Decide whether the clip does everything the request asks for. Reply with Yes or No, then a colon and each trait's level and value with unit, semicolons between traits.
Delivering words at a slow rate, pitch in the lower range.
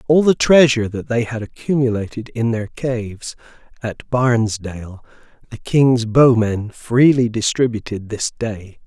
Yes: slow, 130 wpm; low, 115 Hz